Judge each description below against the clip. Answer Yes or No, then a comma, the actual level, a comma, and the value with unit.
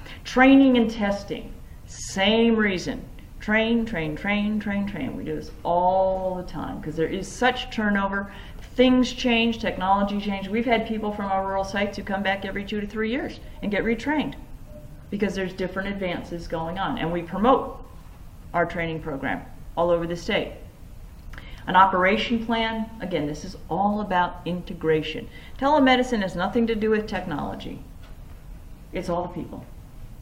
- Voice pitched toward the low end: No, high, 195 Hz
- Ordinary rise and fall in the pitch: Yes, average, 4.6 semitones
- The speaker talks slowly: No, average, 155 wpm